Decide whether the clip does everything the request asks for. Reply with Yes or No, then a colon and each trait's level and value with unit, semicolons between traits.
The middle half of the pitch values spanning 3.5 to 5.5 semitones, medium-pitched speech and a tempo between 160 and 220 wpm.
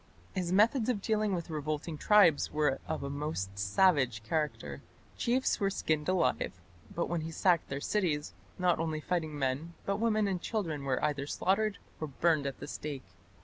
Yes: average, 4.8 semitones; medium, 160 Hz; average, 175 wpm